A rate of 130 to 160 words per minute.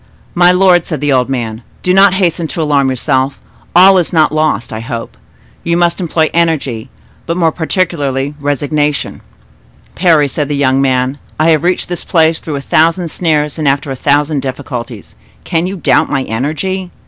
No: average, 175 wpm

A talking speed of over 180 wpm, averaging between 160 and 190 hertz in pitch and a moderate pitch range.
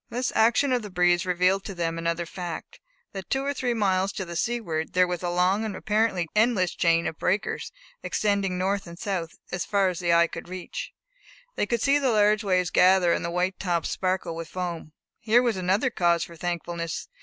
Yes: fast, 205 wpm; medium, 185 Hz; average, 3.4 semitones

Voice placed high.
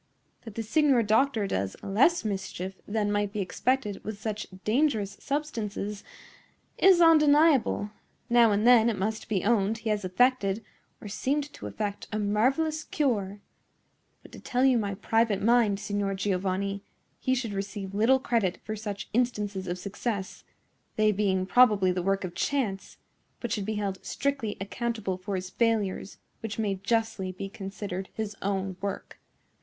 Yes: high, 210 Hz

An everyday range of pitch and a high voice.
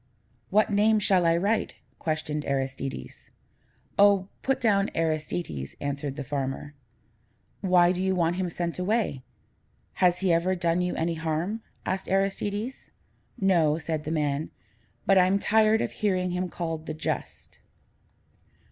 No: average, 3.9 semitones; medium, 175 Hz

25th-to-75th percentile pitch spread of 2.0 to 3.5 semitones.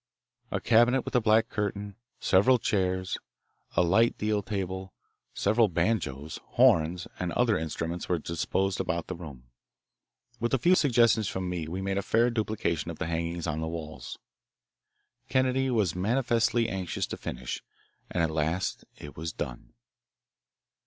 No: average, 5.3 semitones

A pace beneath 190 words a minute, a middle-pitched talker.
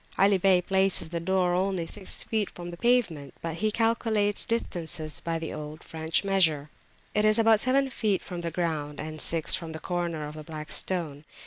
No: average, 195 wpm; medium, 175 Hz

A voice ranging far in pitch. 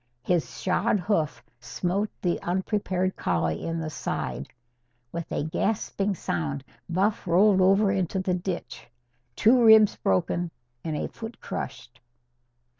No: average, 4.1 semitones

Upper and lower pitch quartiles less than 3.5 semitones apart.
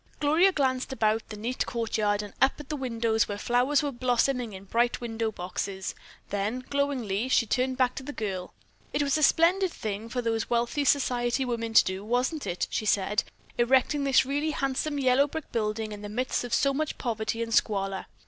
No: average, 4.0 semitones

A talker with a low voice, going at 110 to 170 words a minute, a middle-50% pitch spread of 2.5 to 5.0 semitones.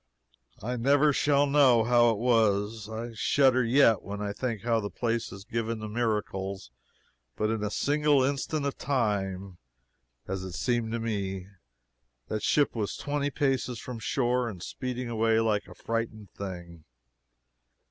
Yes: low, 115 Hz; average, 155 wpm; average, 3.7 semitones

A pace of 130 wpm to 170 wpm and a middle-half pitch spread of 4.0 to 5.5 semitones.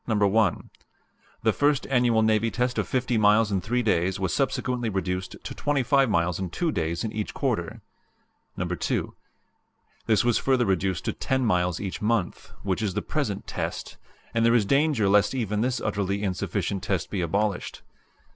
Yes: average, 165 wpm; average, 4.4 semitones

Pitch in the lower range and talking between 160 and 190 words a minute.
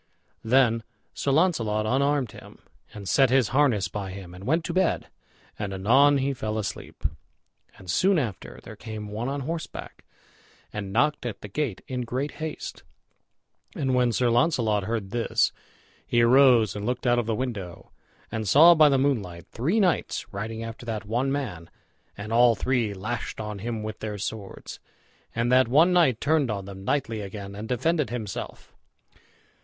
Yes: low, 120 Hz; average, 170 wpm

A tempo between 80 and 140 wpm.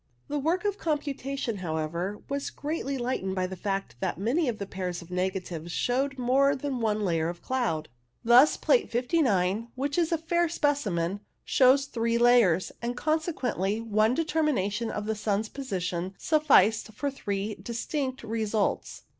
No: average, 155 wpm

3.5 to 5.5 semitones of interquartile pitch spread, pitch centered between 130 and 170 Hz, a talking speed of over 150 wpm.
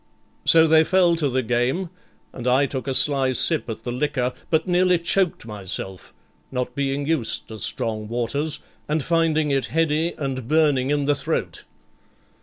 Yes: average, 4.2 semitones; medium, 140 Hz; average, 165 wpm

